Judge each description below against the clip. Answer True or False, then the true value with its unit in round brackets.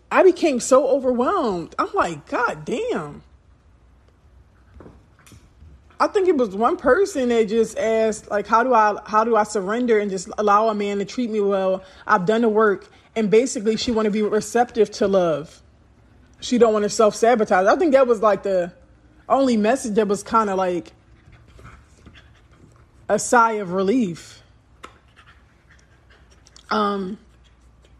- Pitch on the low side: False (210 Hz)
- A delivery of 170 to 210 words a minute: False (150 wpm)